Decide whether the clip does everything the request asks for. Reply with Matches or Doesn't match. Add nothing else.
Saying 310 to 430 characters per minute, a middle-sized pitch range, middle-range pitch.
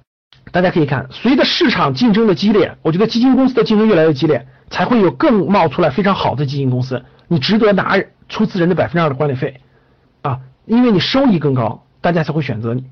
Doesn't match